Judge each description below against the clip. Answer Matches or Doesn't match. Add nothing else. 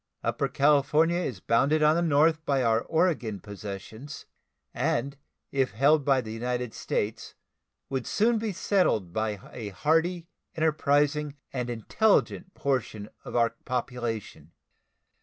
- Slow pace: Matches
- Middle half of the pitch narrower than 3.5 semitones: Doesn't match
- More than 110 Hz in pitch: Matches